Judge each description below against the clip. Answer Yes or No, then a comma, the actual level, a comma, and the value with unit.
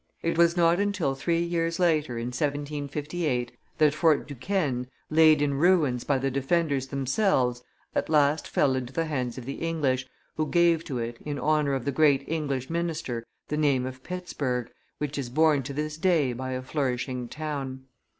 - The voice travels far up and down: No, average, 3.7 semitones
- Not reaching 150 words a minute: No, average, 175 wpm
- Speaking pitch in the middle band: Yes, medium, 145 Hz